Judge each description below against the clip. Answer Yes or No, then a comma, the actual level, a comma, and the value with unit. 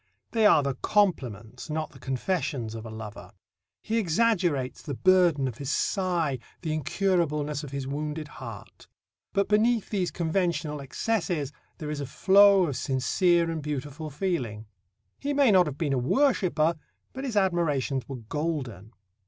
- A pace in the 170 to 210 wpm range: No, average, 155 wpm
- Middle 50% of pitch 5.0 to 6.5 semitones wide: Yes, wide, 5.5 semitones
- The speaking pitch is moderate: Yes, medium, 155 Hz